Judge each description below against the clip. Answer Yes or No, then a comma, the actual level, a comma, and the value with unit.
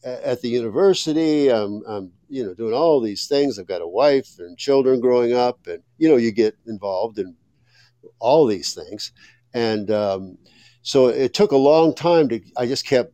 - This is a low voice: Yes, low, 125 Hz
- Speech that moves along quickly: No, average, 185 wpm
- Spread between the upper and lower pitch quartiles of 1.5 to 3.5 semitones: No, average, 4.3 semitones